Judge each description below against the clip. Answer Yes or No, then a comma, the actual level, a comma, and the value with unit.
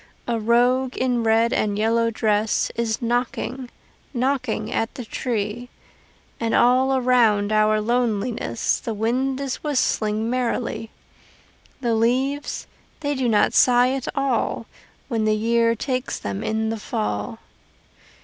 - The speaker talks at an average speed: No, slow, 130 wpm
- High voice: Yes, high, 235 Hz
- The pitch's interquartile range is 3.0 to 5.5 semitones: No, narrow, 2.5 semitones